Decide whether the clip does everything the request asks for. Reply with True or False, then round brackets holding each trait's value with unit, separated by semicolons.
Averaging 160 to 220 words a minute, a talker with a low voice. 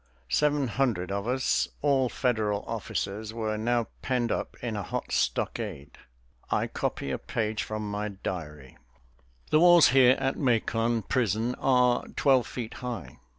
False (145 wpm; 115 Hz)